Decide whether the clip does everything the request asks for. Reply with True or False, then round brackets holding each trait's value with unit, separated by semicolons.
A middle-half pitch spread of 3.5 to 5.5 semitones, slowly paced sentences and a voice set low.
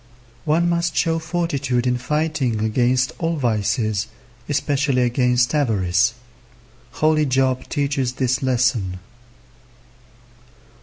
True (3.8 semitones; 95 wpm; 130 Hz)